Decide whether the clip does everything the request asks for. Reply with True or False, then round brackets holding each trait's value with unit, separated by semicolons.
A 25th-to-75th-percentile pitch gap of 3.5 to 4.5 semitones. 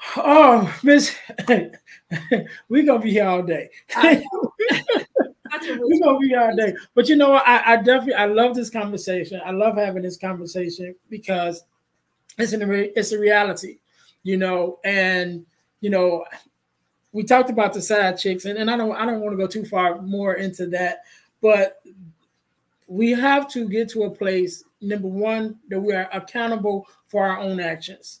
True (4.0 semitones)